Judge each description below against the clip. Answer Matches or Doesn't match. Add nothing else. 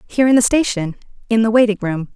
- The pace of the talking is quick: Doesn't match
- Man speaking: Doesn't match